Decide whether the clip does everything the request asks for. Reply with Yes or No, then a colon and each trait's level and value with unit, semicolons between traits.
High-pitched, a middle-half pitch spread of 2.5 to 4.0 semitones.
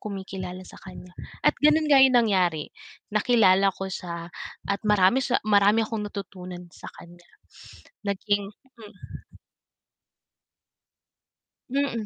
Yes: high, 200 Hz; average, 3.3 semitones